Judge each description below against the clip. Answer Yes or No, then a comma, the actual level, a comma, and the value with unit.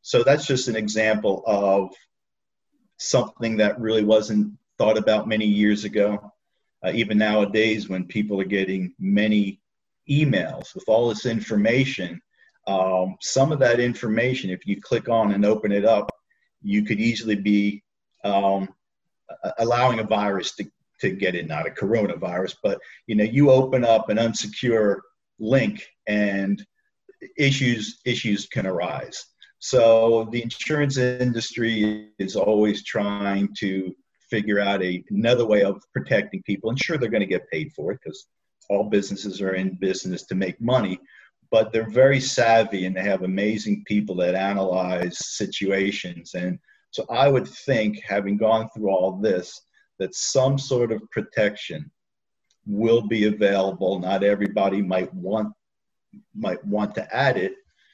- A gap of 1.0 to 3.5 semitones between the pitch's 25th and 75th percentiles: Yes, narrow, 2.6 semitones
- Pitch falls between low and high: No, low, 105 Hz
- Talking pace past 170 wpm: No, average, 150 wpm